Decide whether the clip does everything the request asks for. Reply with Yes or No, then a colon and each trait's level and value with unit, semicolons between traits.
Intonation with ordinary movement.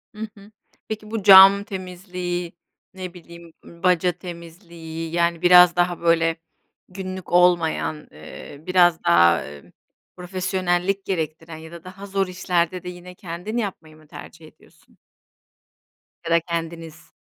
No: narrow, 2.0 semitones